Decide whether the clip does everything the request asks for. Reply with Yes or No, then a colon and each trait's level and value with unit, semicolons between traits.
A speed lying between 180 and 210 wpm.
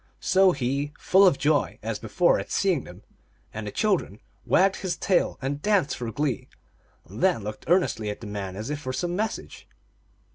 Yes: average, 185 wpm